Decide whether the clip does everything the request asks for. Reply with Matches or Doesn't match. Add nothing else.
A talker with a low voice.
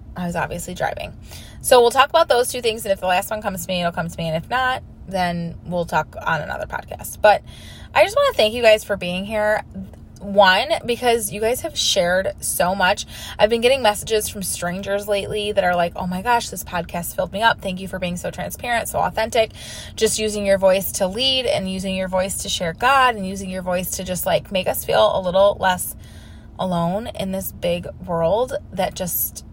Doesn't match